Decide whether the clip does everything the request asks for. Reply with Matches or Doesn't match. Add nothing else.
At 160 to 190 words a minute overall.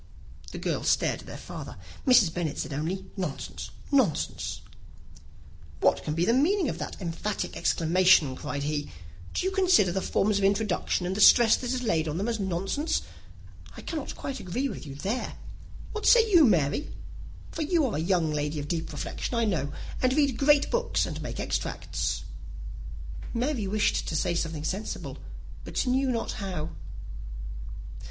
Matches